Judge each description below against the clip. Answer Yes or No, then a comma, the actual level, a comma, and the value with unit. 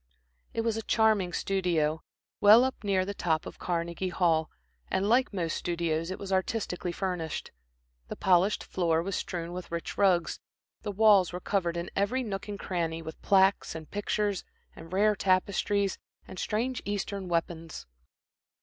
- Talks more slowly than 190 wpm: Yes, average, 160 wpm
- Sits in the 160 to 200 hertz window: Yes, medium, 185 Hz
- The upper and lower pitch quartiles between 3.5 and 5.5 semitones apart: No, average, 3.0 semitones